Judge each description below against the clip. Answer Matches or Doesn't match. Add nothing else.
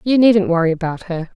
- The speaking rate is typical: Doesn't match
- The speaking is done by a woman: Matches